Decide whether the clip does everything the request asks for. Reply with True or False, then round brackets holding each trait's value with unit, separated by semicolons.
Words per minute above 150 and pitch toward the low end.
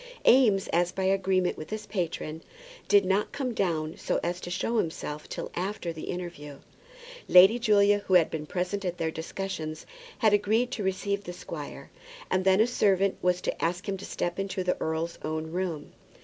False (185 wpm; 185 Hz)